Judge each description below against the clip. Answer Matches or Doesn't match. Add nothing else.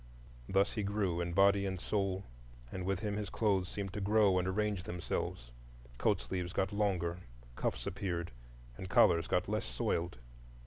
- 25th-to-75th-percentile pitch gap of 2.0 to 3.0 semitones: Matches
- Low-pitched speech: Matches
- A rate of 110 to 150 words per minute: Doesn't match